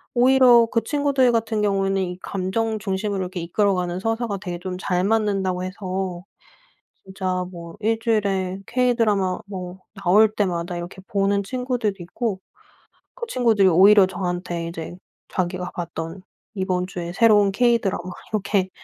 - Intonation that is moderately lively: Yes, average, 3.3 semitones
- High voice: Yes, high, 195 Hz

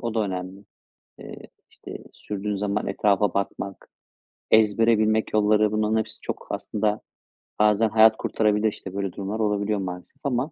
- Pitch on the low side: Yes, low, 105 Hz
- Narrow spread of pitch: Yes, narrow, 1.5 semitones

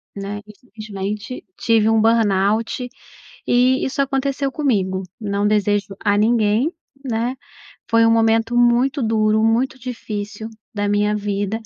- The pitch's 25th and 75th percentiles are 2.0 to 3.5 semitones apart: Yes, average, 2.8 semitones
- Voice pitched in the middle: No, high, 220 Hz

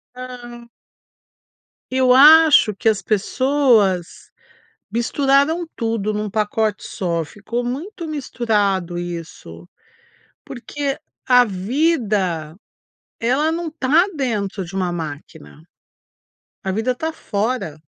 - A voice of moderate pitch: No, high, 230 Hz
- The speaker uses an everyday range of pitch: No, wide, 6.0 semitones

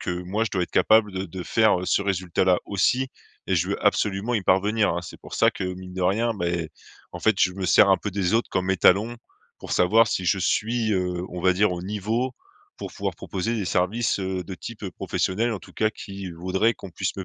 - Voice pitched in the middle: No, very low, 95 Hz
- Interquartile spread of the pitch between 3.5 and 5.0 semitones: No, average, 2.9 semitones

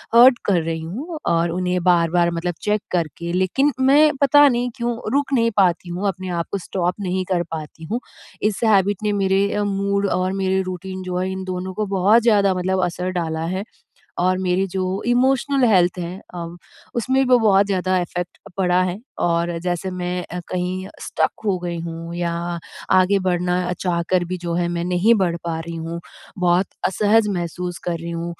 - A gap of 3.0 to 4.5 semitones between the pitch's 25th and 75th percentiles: No, narrow, 2.5 semitones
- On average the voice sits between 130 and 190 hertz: Yes, medium, 185 Hz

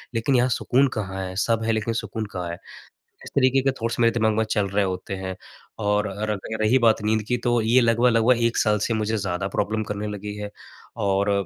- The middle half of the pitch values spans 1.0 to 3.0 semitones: Yes, narrow, 2.4 semitones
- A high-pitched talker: No, low, 110 Hz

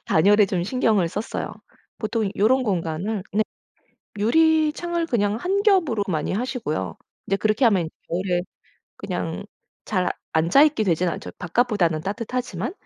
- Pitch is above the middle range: Yes, high, 210 Hz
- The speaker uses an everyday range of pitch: No, wide, 5.7 semitones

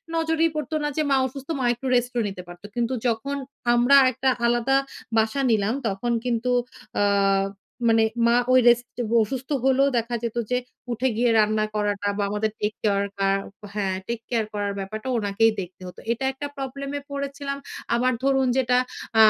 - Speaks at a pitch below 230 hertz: No, high, 240 Hz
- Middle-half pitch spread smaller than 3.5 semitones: No, average, 3.9 semitones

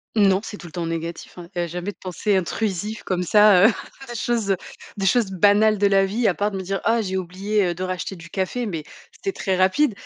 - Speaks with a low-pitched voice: No, high, 195 Hz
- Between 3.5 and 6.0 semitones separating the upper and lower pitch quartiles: No, average, 2.7 semitones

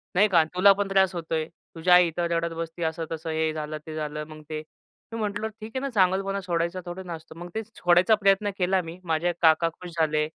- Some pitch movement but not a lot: Yes, average, 3.3 semitones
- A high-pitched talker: No, medium, 175 Hz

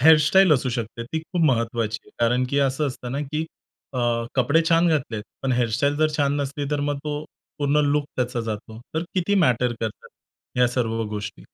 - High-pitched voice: No, low, 135 Hz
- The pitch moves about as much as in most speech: Yes, average, 4.1 semitones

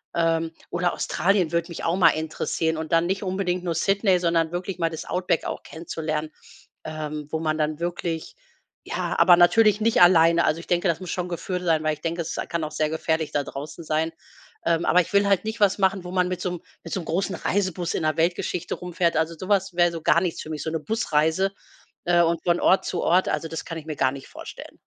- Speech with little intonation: Yes, narrow, 2.2 semitones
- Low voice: No, medium, 170 Hz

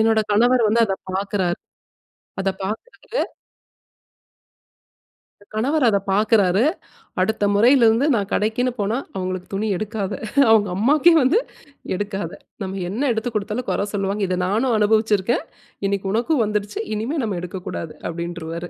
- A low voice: No, high, 210 Hz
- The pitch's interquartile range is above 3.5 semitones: No, average, 3.2 semitones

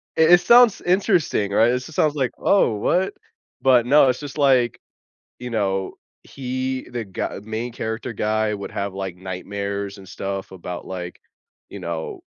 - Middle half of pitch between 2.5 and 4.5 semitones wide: No, average, 5.3 semitones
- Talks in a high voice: No, low, 115 Hz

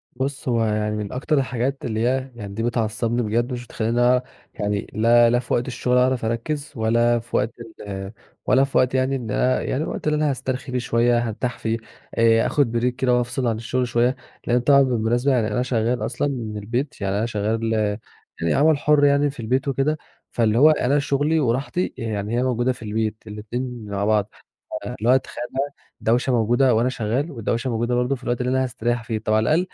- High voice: No, low, 120 Hz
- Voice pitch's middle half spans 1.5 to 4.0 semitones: Yes, narrow, 2.6 semitones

